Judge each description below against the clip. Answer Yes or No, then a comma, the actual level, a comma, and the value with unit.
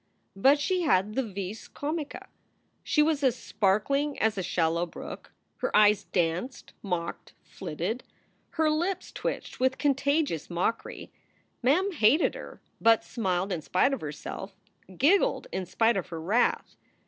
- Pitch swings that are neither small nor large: No, wide, 7.4 semitones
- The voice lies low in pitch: No, high, 225 Hz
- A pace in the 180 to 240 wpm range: No, average, 140 wpm